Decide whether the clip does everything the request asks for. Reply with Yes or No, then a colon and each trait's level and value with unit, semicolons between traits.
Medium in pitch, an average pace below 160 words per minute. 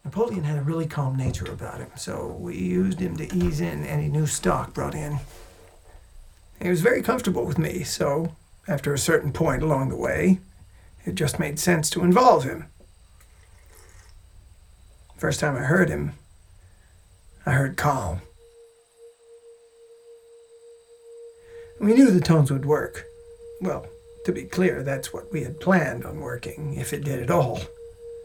Yes: medium, 155 Hz; average, 150 wpm